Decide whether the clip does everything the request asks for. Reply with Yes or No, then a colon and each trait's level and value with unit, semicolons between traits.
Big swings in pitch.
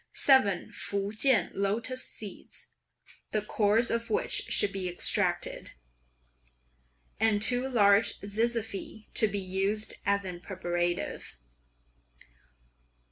No: average, 2.7 semitones